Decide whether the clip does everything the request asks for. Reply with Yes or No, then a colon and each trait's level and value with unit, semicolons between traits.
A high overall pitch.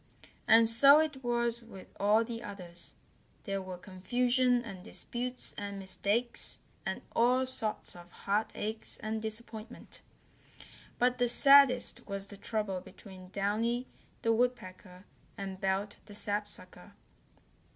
Yes: high, 220 Hz